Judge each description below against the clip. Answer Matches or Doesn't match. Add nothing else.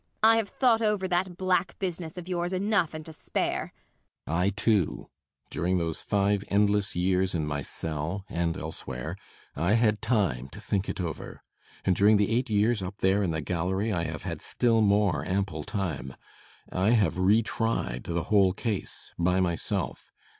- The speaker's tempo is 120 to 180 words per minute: Matches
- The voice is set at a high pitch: Doesn't match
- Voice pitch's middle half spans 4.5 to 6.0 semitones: Matches